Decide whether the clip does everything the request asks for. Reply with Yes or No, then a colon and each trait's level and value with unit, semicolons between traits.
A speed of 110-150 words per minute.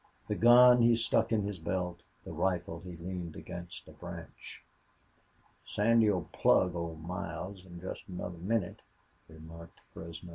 Yes: average, 140 wpm